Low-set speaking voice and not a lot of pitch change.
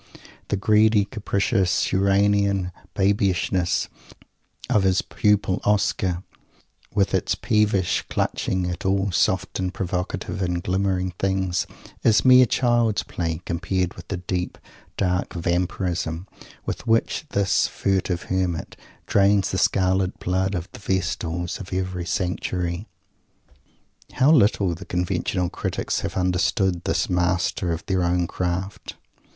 Yes: very low, 95 Hz; narrow, 1.9 semitones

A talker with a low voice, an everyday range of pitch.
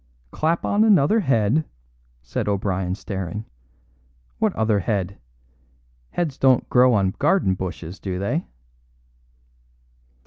No: low, 105 Hz; wide, 7.2 semitones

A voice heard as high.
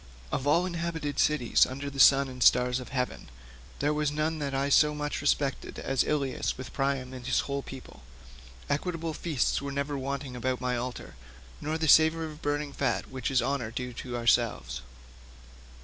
No: medium, 140 Hz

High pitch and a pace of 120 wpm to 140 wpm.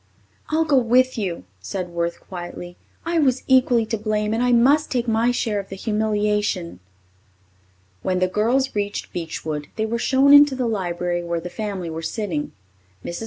No: high, 210 Hz; average, 170 wpm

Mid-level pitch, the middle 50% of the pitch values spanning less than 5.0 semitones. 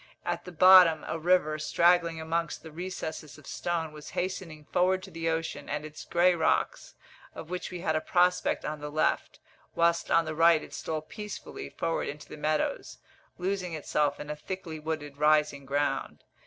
Yes: medium, 160 Hz; narrow, 2.5 semitones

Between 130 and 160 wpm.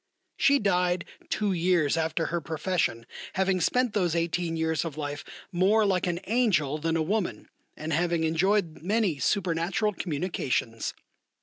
Yes: average, 140 wpm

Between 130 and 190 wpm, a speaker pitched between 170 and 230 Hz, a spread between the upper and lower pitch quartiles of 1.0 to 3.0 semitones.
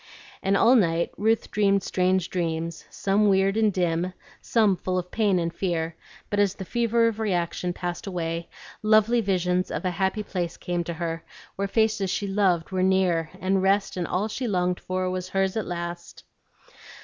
Yes: average, 180 wpm; medium, 185 Hz; average, 2.7 semitones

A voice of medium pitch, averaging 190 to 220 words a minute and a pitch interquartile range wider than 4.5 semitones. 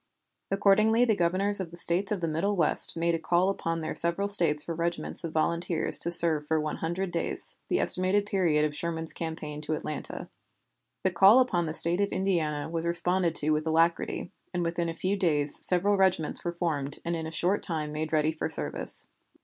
No: medium, 170 Hz; average, 200 wpm; average, 2.9 semitones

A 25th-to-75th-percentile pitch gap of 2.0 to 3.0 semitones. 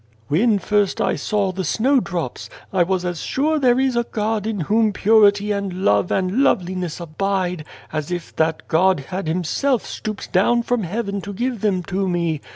No: average, 3.8 semitones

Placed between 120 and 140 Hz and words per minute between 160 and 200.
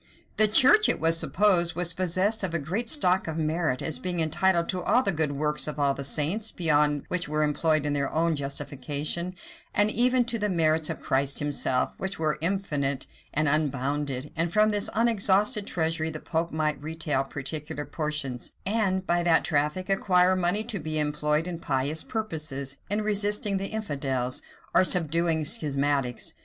No: medium, 160 Hz; average, 170 wpm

